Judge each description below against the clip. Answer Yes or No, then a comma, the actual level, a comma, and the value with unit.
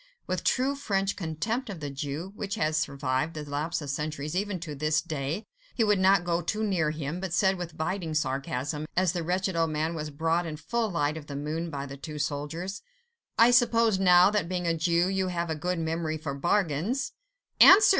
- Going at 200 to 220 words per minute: Yes, fast, 205 wpm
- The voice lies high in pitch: No, medium, 165 Hz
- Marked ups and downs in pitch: No, average, 3.9 semitones